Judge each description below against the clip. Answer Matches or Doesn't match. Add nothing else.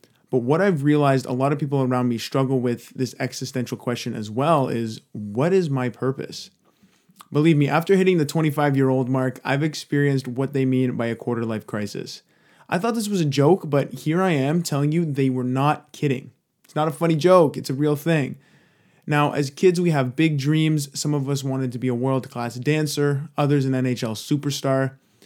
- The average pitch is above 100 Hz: Matches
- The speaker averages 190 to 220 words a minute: Matches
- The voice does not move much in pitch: Doesn't match